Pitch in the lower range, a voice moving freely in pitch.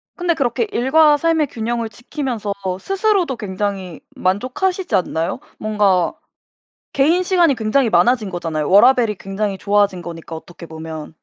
No: high, 220 Hz; wide, 7.3 semitones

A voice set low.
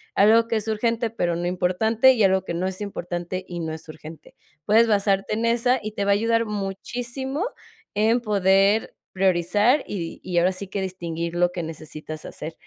No: high, 195 Hz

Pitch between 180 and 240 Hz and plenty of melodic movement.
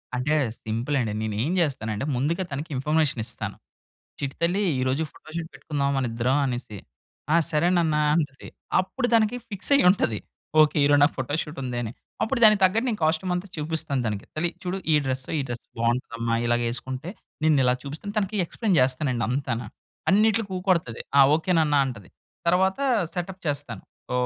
No: medium, 145 Hz; wide, 5.9 semitones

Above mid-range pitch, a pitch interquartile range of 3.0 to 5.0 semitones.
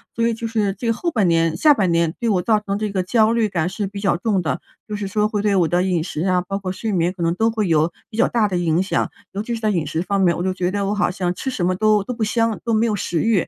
Yes: high, 200 Hz; average, 3.5 semitones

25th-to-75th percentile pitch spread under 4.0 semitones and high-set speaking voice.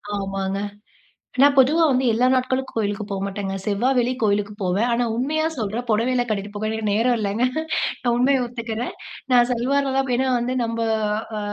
Yes: average, 3.6 semitones; high, 235 Hz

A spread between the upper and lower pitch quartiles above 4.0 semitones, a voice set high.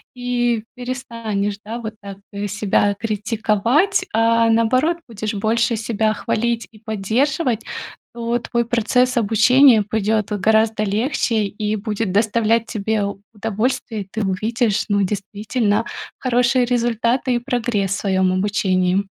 No: narrow, 2.4 semitones; high, 220 Hz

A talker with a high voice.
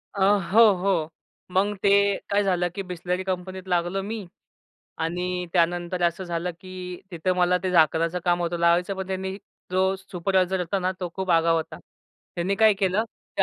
No: medium, 180 Hz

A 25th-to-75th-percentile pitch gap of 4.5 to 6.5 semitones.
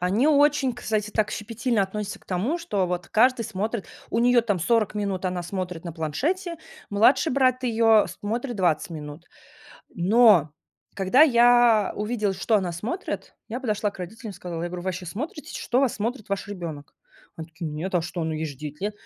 Yes: average, 5.2 semitones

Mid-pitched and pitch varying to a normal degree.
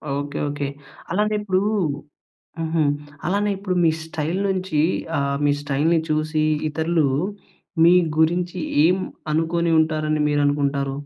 Yes: medium, 160 Hz; average, 3.2 semitones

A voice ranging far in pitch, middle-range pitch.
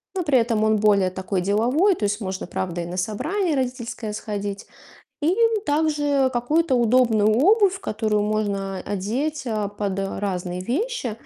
No: wide, 5.9 semitones; high, 220 Hz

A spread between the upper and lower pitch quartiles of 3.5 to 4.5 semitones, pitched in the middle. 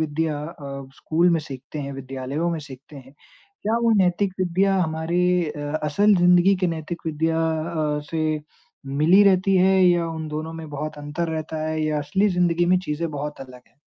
No: average, 3.0 semitones; medium, 160 Hz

